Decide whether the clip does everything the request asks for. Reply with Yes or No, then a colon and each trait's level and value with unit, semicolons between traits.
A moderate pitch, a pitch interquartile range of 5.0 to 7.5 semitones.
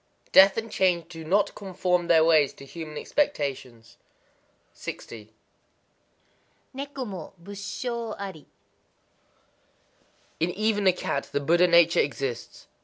Yes: medium, 175 Hz; wide, 5.5 semitones